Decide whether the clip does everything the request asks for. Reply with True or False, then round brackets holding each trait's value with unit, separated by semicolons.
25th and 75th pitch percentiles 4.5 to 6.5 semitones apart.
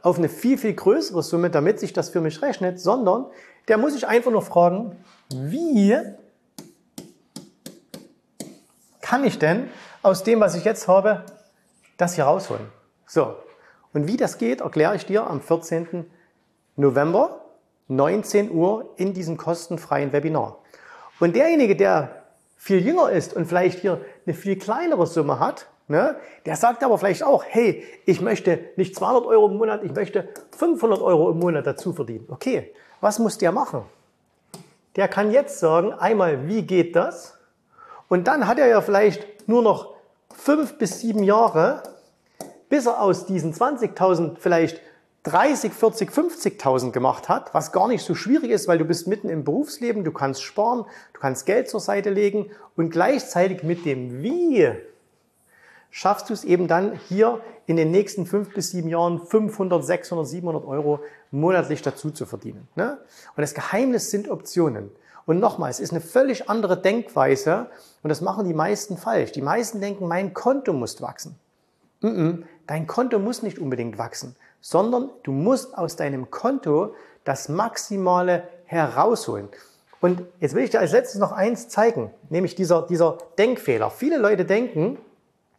True (5.2 semitones)